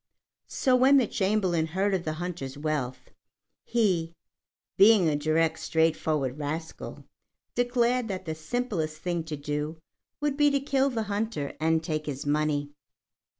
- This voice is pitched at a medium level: Yes, medium, 165 Hz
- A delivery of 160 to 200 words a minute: No, average, 145 wpm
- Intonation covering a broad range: Yes, wide, 6.3 semitones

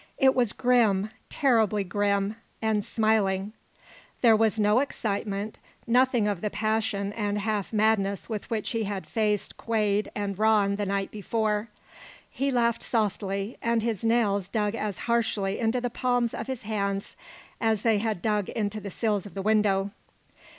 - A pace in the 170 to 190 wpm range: No, average, 155 wpm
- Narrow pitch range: Yes, narrow, 2.1 semitones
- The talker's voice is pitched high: Yes, high, 215 Hz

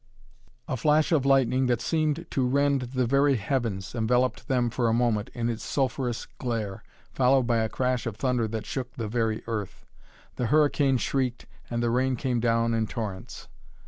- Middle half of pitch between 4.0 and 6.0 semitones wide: No, narrow, 2.5 semitones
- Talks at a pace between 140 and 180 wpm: Yes, average, 175 wpm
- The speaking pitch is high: No, low, 125 Hz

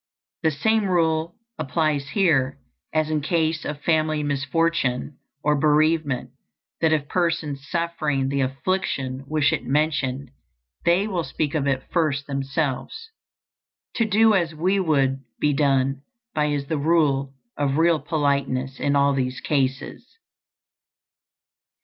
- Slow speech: Yes, slow, 130 wpm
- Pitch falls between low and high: Yes, medium, 150 Hz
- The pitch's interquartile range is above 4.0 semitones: No, average, 3.1 semitones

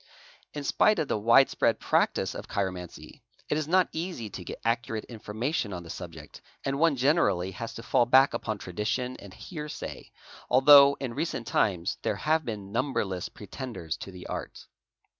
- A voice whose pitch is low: Yes, low, 115 Hz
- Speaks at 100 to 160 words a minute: No, average, 180 wpm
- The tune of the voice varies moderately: No, wide, 5.9 semitones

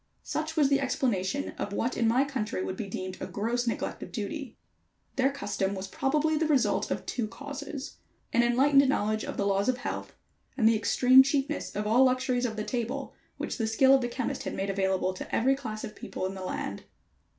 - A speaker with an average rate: No, fast, 210 wpm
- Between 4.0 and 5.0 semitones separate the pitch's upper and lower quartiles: Yes, average, 4.4 semitones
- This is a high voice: Yes, high, 245 Hz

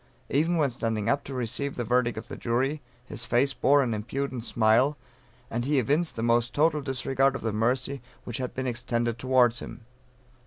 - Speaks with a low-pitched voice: Yes, low, 125 Hz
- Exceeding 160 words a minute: Yes, average, 190 wpm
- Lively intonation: No, average, 2.8 semitones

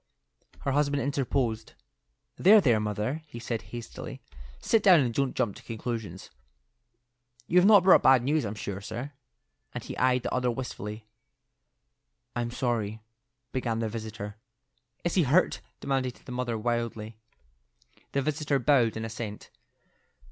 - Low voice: Yes, low, 120 Hz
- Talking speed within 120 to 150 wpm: Yes, average, 140 wpm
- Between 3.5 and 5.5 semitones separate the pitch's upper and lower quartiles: Yes, average, 3.9 semitones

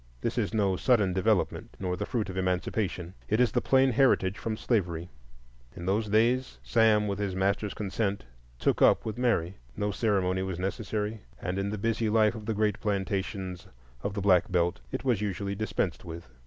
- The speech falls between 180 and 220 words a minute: Yes, average, 185 wpm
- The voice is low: Yes, low, 100 Hz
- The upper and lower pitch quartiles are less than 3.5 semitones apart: Yes, average, 2.7 semitones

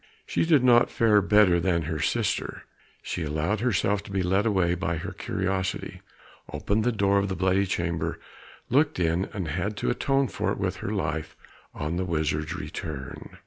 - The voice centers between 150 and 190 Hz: No, very low, 95 Hz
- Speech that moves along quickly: No, average, 180 wpm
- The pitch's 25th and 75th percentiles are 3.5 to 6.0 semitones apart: Yes, average, 3.9 semitones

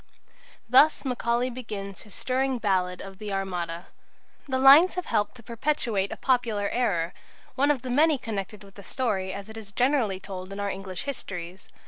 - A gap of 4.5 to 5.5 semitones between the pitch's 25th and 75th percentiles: Yes, average, 4.8 semitones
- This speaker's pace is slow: No, average, 175 wpm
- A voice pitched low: No, high, 215 Hz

